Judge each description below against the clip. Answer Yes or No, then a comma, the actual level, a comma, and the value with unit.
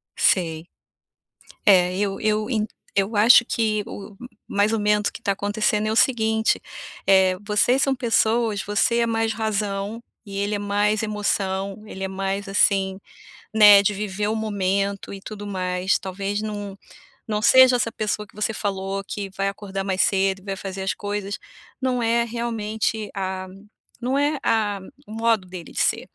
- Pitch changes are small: Yes, narrow, 2.1 semitones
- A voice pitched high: Yes, high, 205 Hz